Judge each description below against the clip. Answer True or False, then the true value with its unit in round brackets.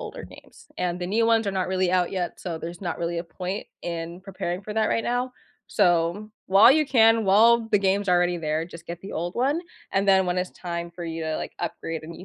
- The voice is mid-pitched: True (180 Hz)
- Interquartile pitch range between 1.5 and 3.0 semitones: False (3.5 semitones)